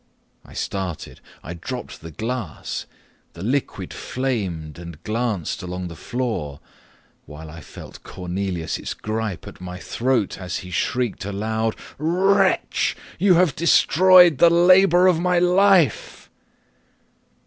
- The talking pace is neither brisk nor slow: No, slow, 120 wpm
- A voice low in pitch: Yes, low, 110 Hz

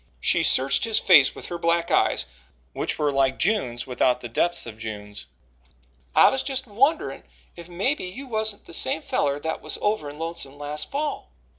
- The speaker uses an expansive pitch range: Yes, wide, 7.9 semitones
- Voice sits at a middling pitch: Yes, medium, 170 Hz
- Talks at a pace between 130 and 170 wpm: No, average, 185 wpm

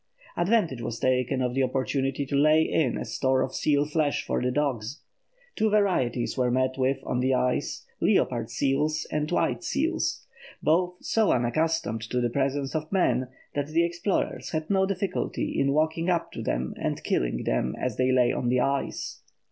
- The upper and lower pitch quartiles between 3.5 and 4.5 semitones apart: Yes, average, 3.9 semitones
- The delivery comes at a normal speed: Yes, average, 180 wpm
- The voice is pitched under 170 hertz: Yes, low, 135 Hz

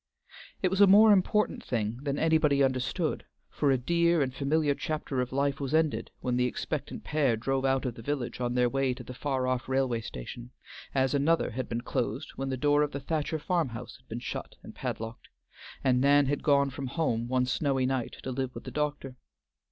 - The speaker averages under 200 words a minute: No, fast, 205 wpm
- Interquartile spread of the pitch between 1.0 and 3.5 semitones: Yes, average, 2.8 semitones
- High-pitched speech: No, low, 135 Hz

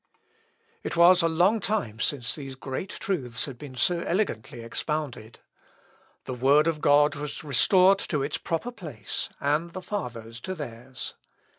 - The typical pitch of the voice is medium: Yes, medium, 150 Hz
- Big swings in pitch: Yes, wide, 5.9 semitones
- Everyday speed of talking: Yes, average, 155 wpm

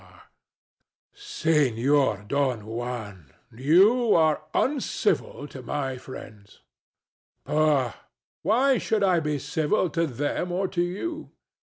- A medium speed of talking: No, slow, 120 wpm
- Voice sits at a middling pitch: Yes, medium, 150 Hz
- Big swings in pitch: Yes, wide, 7.0 semitones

